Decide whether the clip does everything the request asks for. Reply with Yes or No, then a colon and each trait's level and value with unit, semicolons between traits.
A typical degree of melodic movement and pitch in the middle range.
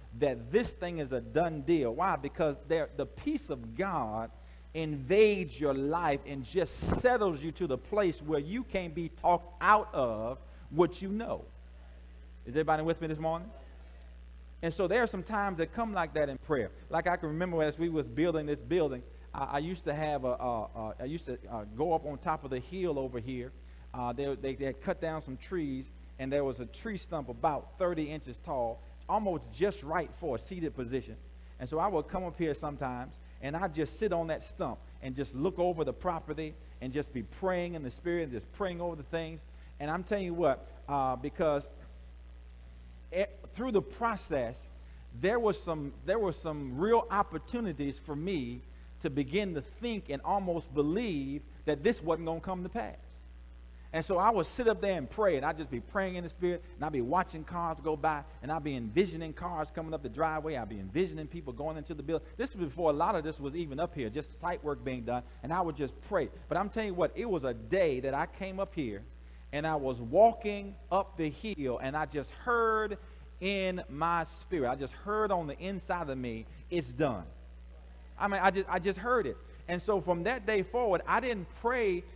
No: wide, 5.9 semitones; medium, 155 Hz